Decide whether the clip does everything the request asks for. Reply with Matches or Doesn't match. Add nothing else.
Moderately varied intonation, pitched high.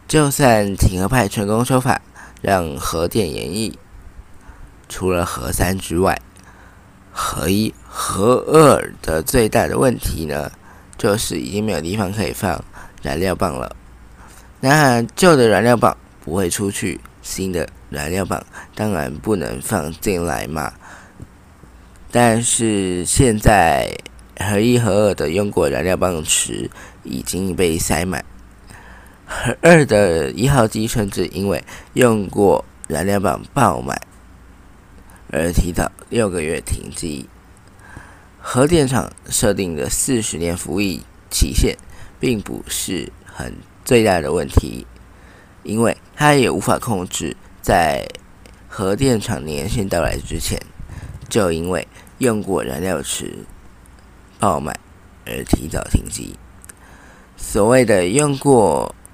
Doesn't match